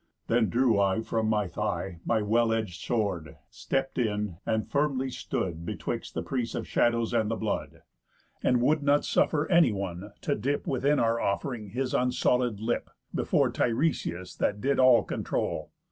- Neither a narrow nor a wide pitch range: Yes, average, 3.9 semitones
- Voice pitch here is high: No, low, 115 Hz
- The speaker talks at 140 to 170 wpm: Yes, average, 160 wpm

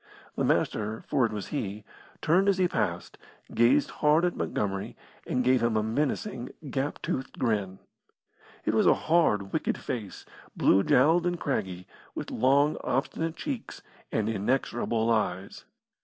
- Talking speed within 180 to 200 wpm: No, average, 145 wpm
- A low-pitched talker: Yes, low, 125 Hz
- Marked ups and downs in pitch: Yes, wide, 6.0 semitones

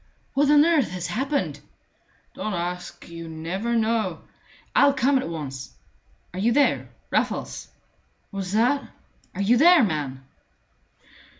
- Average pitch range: No, wide, 8.0 semitones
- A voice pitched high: Yes, high, 215 Hz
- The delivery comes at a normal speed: No, slow, 130 wpm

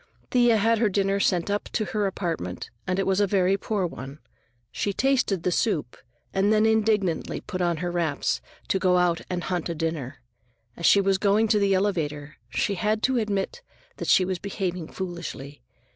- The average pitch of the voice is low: No, high, 190 Hz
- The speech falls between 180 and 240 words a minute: Yes, average, 190 wpm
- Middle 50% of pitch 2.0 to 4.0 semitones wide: Yes, average, 3.2 semitones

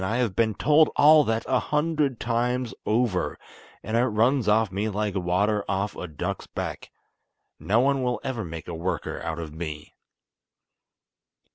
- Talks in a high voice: No, low, 110 Hz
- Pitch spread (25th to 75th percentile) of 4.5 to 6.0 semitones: Yes, average, 5.2 semitones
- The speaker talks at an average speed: Yes, average, 160 wpm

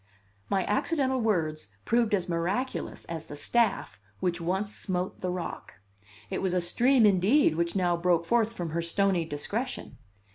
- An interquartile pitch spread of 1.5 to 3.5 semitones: No, average, 4.5 semitones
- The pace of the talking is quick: No, average, 155 wpm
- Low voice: No, medium, 185 Hz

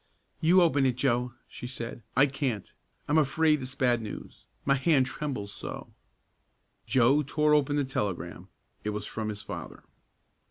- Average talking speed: Yes, average, 155 wpm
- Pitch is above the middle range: No, low, 130 Hz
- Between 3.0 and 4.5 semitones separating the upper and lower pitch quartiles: Yes, average, 3.9 semitones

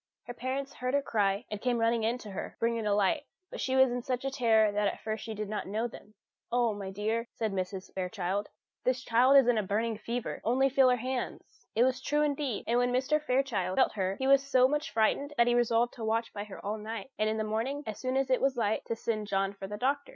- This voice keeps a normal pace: No, fast, 255 wpm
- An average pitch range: Yes, average, 3.5 semitones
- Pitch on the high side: Yes, high, 230 Hz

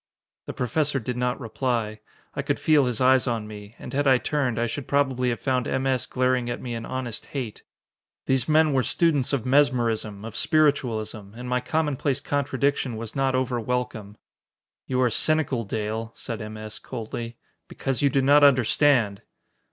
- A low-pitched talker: Yes, low, 125 Hz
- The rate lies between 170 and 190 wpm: Yes, average, 175 wpm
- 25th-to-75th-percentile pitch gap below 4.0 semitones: Yes, average, 3.3 semitones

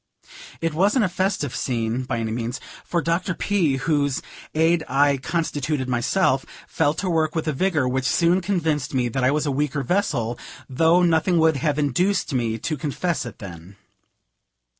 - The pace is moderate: Yes, average, 170 wpm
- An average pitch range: Yes, average, 4.7 semitones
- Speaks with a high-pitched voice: No, medium, 150 Hz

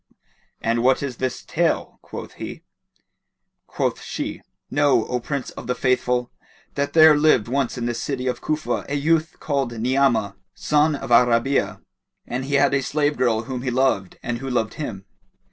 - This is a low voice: Yes, low, 130 Hz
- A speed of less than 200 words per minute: Yes, average, 175 wpm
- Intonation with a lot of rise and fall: No, average, 2.9 semitones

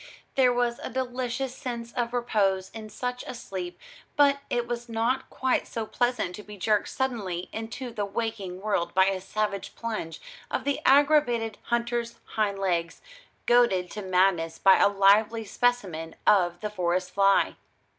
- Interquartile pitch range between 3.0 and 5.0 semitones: Yes, average, 4.1 semitones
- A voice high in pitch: Yes, high, 220 Hz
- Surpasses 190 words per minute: No, average, 155 wpm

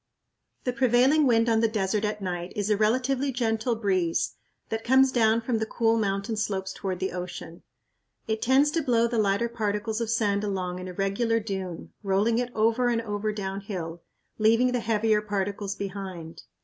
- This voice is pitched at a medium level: No, high, 215 Hz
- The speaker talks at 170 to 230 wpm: Yes, average, 175 wpm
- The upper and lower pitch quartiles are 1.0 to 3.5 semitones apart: Yes, average, 2.9 semitones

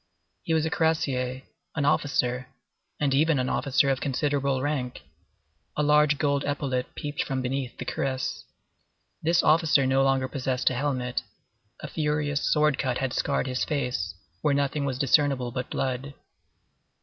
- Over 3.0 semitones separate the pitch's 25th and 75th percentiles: No, narrow, 2.4 semitones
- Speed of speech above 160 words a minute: No, average, 150 wpm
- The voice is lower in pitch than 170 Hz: Yes, medium, 140 Hz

